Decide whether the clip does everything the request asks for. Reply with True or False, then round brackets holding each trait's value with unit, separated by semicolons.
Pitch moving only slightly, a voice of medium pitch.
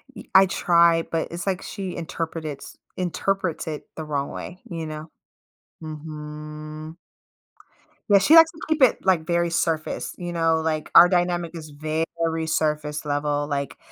True (2.3 semitones; 160 Hz)